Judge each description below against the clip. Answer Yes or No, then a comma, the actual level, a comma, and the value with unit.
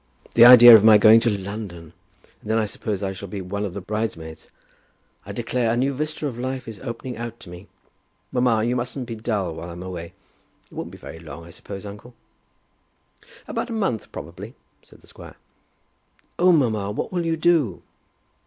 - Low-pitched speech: Yes, low, 110 Hz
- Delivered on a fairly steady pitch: No, average, 4.2 semitones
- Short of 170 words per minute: No, average, 190 wpm